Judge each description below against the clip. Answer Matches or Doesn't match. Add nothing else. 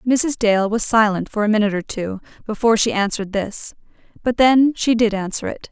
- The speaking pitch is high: Matches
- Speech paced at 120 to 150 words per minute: Doesn't match